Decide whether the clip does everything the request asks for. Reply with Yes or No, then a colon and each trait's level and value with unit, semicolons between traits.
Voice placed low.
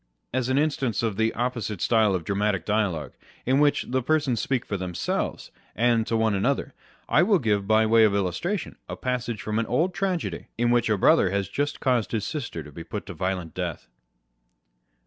Yes: low, 110 Hz